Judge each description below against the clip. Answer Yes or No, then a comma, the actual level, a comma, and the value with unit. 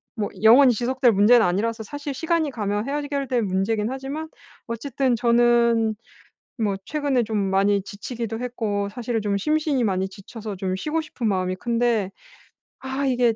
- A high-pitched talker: Yes, high, 230 Hz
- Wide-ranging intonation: No, average, 4.3 semitones